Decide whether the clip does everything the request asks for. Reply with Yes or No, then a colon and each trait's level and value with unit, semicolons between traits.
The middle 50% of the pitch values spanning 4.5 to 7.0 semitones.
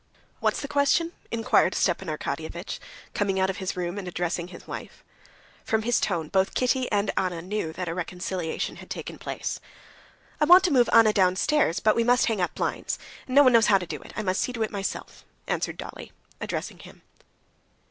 Yes: average, 4.9 semitones